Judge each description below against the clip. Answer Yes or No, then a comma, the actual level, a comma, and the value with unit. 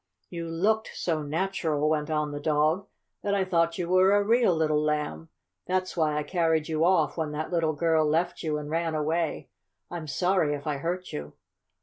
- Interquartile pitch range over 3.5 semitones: No, average, 2.9 semitones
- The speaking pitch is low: No, medium, 160 Hz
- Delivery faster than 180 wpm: Yes, average, 195 wpm